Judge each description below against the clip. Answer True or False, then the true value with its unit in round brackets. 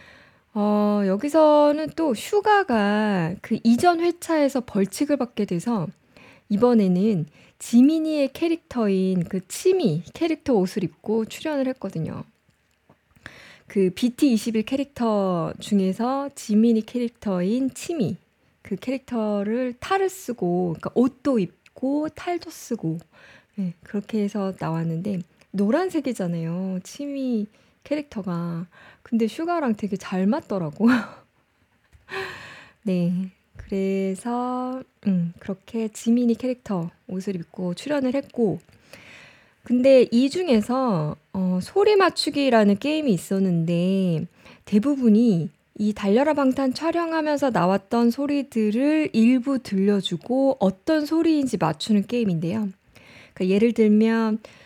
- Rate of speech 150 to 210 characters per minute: False (240 characters per minute)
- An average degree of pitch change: False (5.9 semitones)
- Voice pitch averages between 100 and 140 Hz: False (220 Hz)